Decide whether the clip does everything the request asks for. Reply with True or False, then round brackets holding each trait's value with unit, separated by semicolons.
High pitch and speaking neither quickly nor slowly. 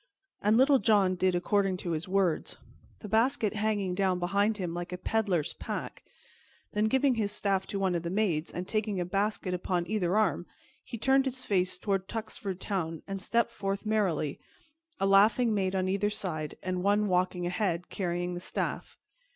True (195 Hz; 180 wpm)